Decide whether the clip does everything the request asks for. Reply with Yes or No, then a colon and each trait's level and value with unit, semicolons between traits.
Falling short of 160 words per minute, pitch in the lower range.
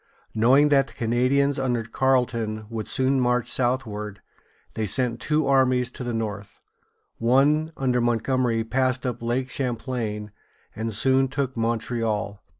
Yes: average, 150 wpm; low, 125 Hz